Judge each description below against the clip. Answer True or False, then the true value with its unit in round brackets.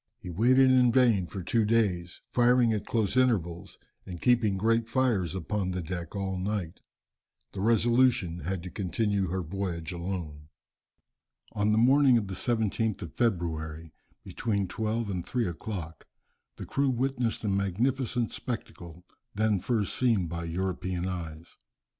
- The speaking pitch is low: True (100 Hz)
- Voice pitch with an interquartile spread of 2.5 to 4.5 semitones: False (4.9 semitones)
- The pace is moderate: True (145 wpm)